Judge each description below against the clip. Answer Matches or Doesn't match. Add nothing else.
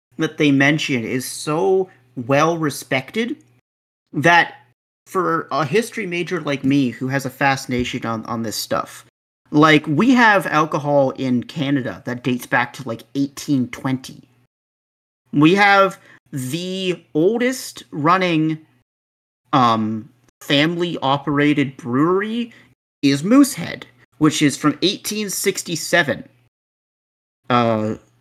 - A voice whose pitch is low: Doesn't match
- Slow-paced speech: Matches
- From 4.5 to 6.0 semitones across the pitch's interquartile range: Matches